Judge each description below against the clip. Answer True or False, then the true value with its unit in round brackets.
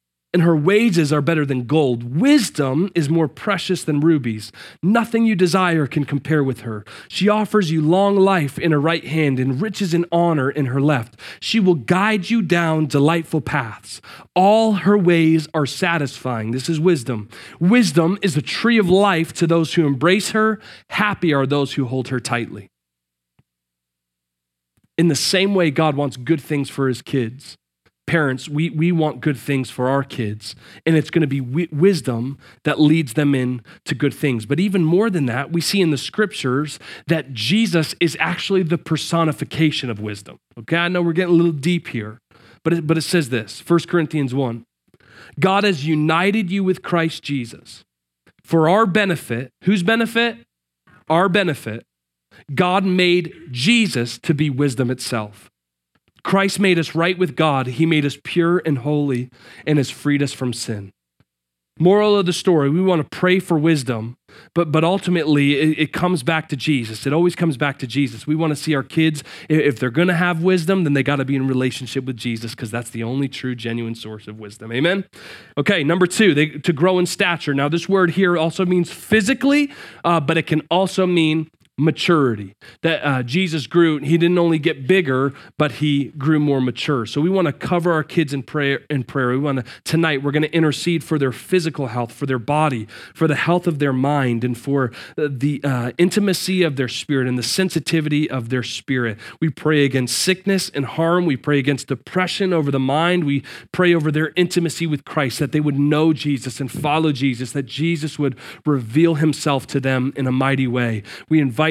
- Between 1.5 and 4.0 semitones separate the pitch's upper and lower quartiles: False (4.7 semitones)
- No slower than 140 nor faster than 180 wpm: False (190 wpm)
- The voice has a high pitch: False (155 Hz)